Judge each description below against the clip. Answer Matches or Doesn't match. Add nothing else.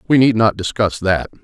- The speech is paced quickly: Matches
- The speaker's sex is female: Doesn't match